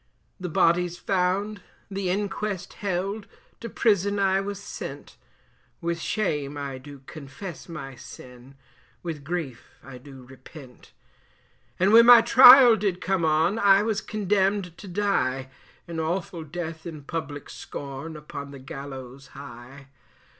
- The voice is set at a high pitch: No, medium, 170 Hz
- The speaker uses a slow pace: Yes, slow, 130 wpm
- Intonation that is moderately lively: No, wide, 6.0 semitones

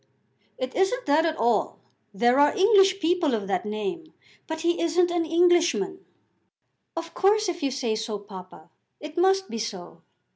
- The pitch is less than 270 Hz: No, very high, 320 Hz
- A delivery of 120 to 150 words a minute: No, average, 160 wpm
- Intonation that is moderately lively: No, wide, 7.8 semitones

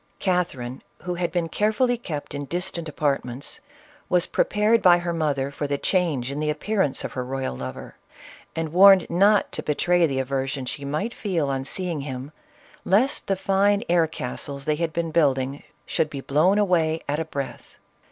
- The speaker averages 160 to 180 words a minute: Yes, average, 175 wpm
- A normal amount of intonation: Yes, average, 4.5 semitones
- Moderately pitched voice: Yes, medium, 160 Hz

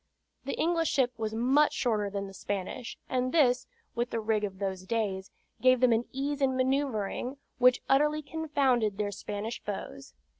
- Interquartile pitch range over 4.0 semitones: Yes, average, 4.6 semitones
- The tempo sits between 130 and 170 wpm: Yes, average, 165 wpm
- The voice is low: No, high, 245 Hz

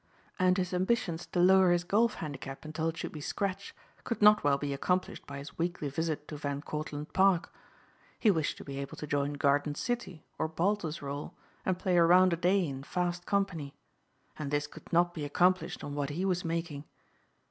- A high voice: No, medium, 165 Hz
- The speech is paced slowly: No, average, 195 wpm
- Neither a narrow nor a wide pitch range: Yes, average, 4.1 semitones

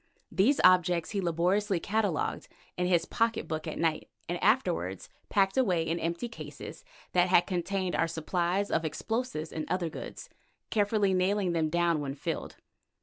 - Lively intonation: No, average, 3.2 semitones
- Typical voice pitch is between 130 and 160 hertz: No, medium, 180 Hz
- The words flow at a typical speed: Yes, average, 155 wpm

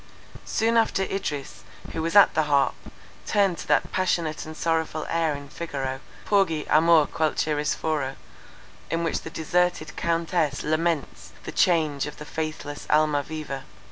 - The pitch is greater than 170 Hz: No, medium, 155 Hz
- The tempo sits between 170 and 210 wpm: No, average, 140 wpm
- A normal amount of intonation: No, narrow, 2.2 semitones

